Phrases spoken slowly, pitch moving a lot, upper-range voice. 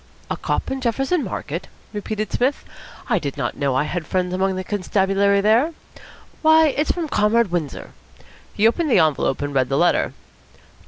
No: average, 170 wpm; wide, 6.4 semitones; high, 200 Hz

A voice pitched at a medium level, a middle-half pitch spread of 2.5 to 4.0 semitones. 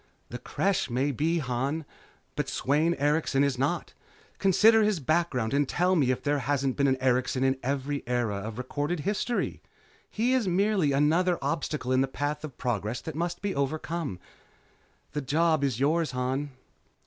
No: medium, 145 Hz; average, 4.4 semitones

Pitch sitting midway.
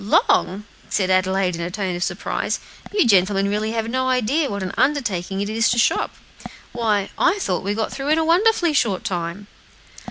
No: high, 210 Hz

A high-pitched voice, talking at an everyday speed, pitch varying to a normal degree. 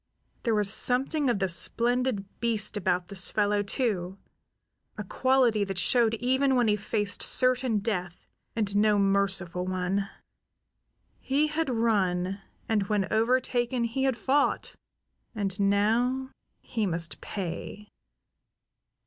No: high, 210 Hz; slow, 125 wpm; average, 3.9 semitones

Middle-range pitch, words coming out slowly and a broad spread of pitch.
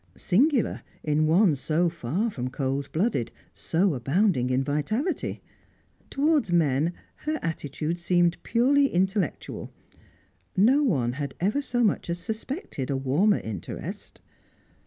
Yes: medium, 175 Hz; slow, 120 wpm; wide, 7.7 semitones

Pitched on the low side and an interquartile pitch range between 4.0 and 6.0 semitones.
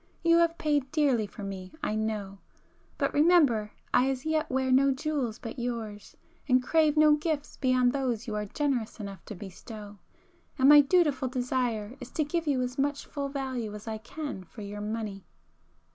No: very high, 255 Hz; average, 5.1 semitones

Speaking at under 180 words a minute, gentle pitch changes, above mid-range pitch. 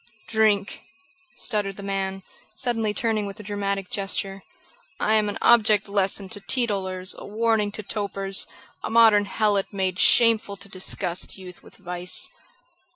Yes: average, 145 wpm; narrow, 1.9 semitones; high, 200 Hz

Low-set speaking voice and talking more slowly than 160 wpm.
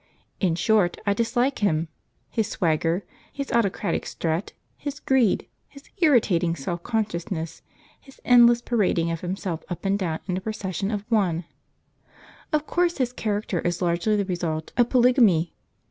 No: high, 200 Hz; average, 145 wpm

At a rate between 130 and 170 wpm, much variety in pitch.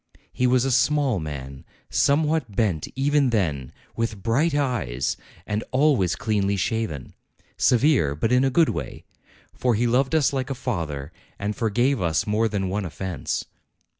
Yes: average, 160 wpm; wide, 6.3 semitones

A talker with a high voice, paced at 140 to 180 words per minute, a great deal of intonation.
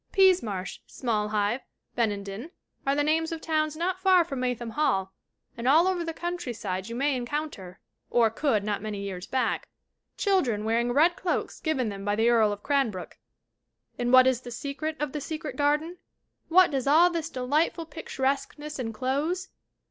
Yes: very high, 265 Hz; average, 165 wpm; wide, 6.0 semitones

